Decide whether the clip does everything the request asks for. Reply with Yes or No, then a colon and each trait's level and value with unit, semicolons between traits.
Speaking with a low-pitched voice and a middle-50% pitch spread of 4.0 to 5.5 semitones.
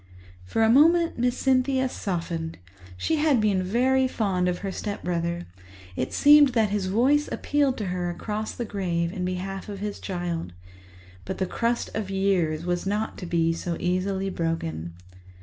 No: high, 195 Hz; average, 5.2 semitones